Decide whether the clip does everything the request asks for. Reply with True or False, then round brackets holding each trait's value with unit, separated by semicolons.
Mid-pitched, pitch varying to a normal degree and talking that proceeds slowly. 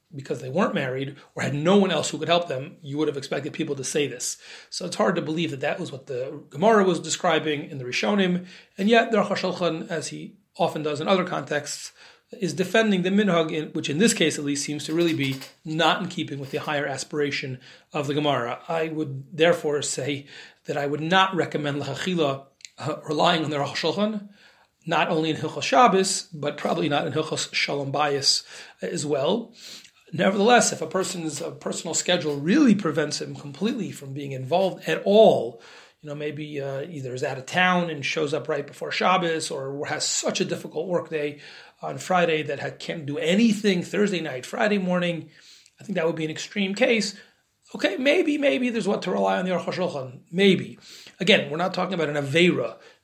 False (160 Hz; 4.1 semitones; 205 wpm)